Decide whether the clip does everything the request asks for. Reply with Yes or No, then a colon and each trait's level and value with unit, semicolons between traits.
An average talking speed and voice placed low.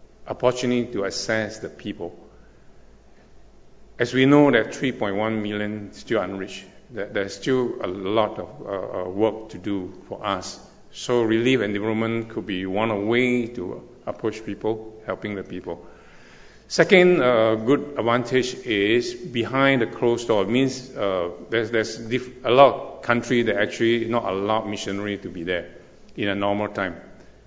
Yes: average, 155 wpm; low, 115 Hz